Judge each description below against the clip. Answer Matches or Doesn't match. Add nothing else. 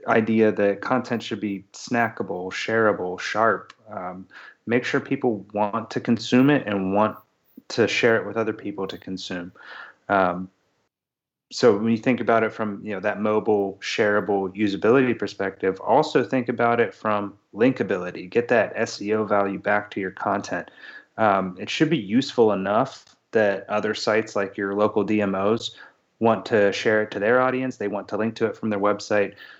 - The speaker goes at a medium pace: Matches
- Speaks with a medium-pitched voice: Doesn't match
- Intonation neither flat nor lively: Doesn't match